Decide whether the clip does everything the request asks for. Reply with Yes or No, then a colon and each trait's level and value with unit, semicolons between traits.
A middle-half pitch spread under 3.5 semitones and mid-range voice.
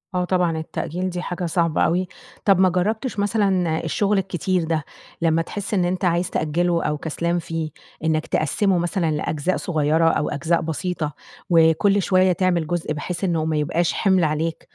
Yes: narrow, 2.5 semitones; medium, 170 Hz